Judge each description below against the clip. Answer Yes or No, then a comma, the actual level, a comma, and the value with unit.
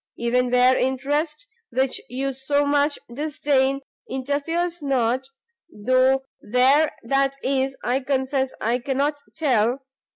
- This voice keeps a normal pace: No, slow, 110 wpm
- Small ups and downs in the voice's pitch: Yes, narrow, 1.9 semitones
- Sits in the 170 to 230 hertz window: No, very high, 270 Hz